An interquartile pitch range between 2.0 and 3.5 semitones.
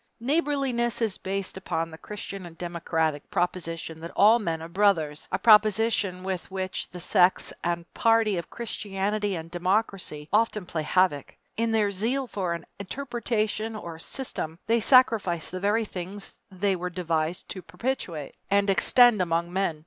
No: average, 4.2 semitones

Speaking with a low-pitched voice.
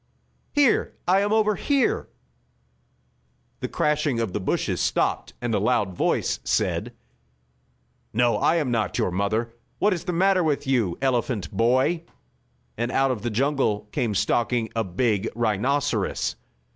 Yes: low, 120 Hz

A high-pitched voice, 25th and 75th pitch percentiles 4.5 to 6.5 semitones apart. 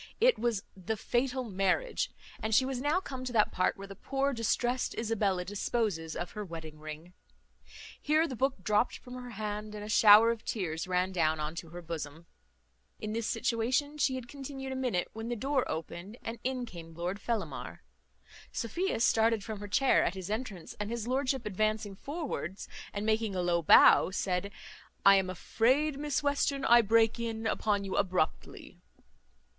Yes: high, 220 Hz; average, 5.1 semitones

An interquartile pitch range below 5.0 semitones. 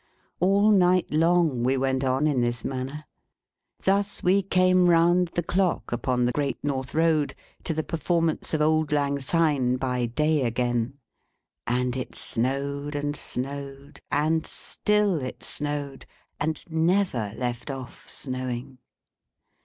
Yes: average, 4.4 semitones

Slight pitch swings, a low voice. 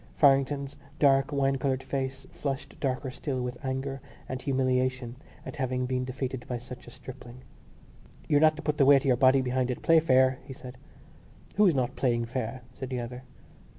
Yes: narrow, 1.4 semitones; low, 130 Hz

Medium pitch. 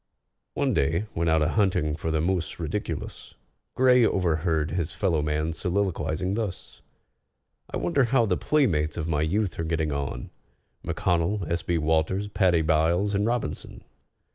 No: very low, 85 Hz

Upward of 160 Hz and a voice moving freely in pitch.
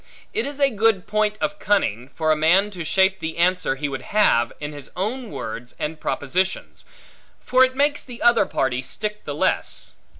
Yes: high, 190 Hz; wide, 6.3 semitones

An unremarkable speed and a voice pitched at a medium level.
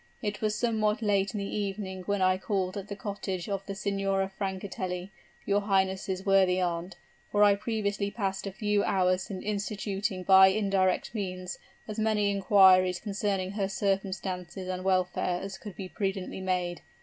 No: average, 160 wpm; high, 195 Hz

